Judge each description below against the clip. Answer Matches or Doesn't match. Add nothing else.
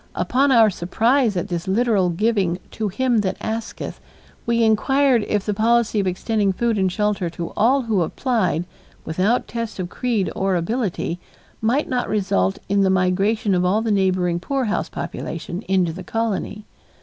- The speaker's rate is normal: Matches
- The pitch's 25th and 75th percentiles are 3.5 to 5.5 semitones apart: Matches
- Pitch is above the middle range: Matches